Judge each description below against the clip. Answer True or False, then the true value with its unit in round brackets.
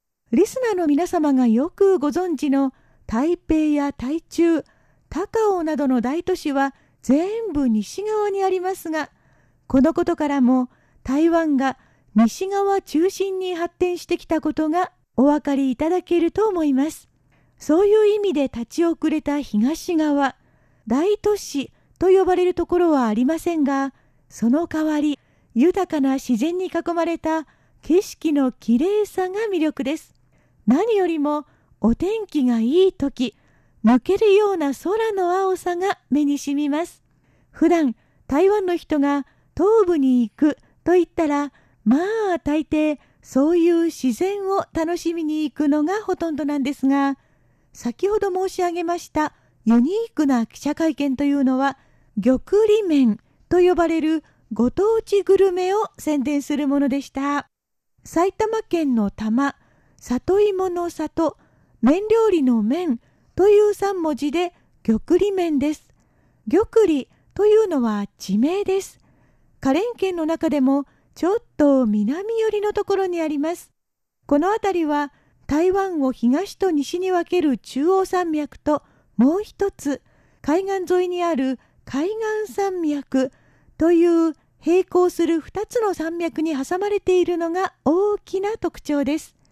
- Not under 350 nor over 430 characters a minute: False (250 characters per minute)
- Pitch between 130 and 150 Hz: False (320 Hz)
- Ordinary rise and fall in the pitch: True (4.8 semitones)